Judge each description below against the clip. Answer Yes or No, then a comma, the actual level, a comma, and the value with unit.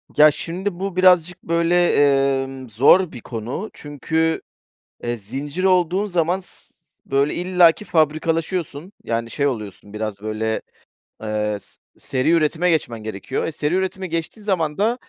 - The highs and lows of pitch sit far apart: Yes, wide, 6.2 semitones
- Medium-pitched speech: Yes, medium, 160 Hz